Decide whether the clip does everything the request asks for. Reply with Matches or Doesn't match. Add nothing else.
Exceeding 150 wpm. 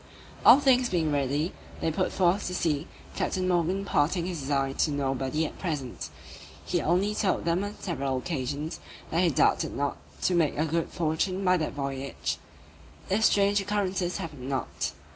Matches